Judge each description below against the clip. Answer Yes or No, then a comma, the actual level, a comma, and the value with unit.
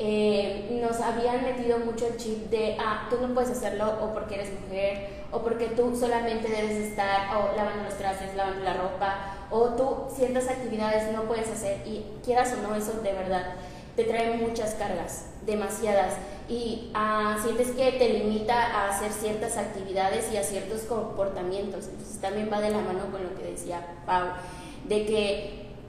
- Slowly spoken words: No, average, 175 wpm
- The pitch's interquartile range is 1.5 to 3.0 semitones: Yes, average, 2.7 semitones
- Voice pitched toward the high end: Yes, high, 215 Hz